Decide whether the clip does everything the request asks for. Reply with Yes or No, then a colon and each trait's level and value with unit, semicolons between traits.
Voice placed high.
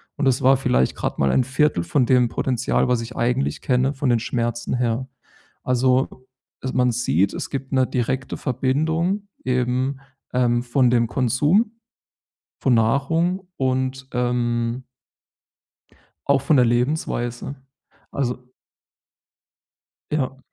No: low, 130 Hz